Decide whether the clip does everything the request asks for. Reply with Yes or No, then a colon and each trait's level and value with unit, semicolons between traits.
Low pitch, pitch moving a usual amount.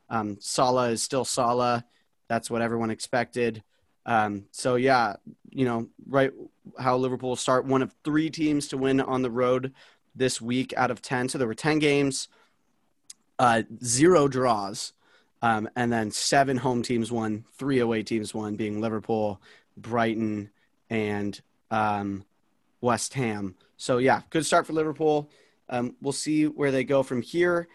Yes: low, 125 Hz; average, 3.1 semitones